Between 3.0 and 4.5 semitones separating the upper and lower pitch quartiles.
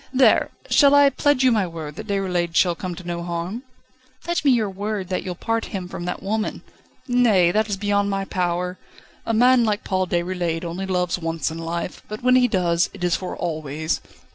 Yes: average, 3.9 semitones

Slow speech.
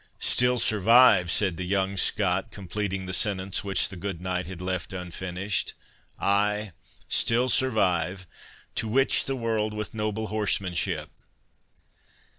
Yes: slow, 120 wpm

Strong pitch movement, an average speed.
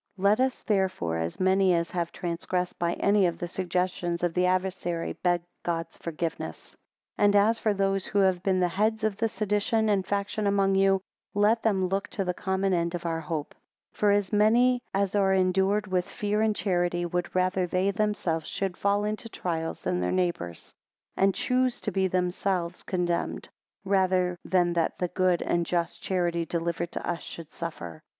No: narrow, 2.6 semitones; average, 185 wpm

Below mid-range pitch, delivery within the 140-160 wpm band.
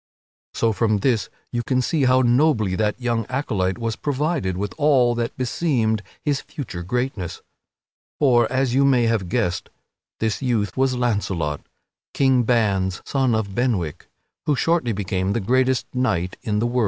Yes: low, 120 Hz; average, 155 wpm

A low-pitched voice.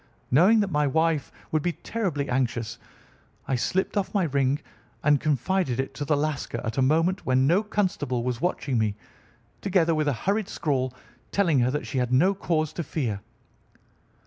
No: medium, 150 Hz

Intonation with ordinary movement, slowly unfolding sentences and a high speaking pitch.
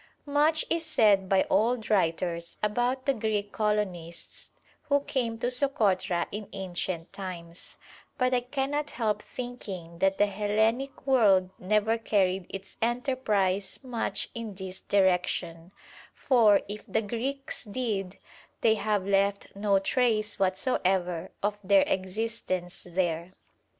Yes: average, 4.2 semitones; slow, 125 wpm; high, 205 Hz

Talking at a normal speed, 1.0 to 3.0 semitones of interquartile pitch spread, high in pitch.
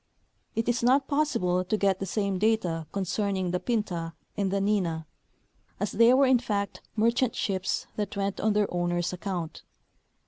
No: average, 165 wpm; average, 3.5 semitones; high, 200 Hz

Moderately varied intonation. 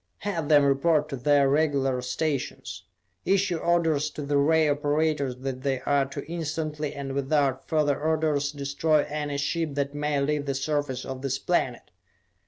No: narrow, 2.1 semitones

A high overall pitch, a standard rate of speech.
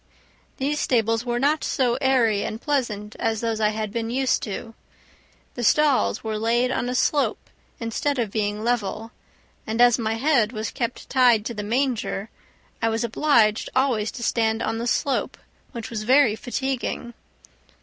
Yes: high, 230 Hz; average, 165 wpm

